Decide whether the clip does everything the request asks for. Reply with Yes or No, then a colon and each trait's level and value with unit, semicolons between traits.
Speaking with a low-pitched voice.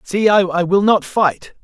No: high, 190 Hz